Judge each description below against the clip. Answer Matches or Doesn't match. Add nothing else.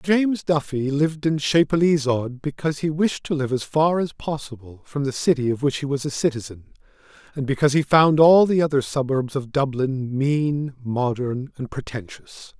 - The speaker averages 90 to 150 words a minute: Doesn't match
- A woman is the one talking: Doesn't match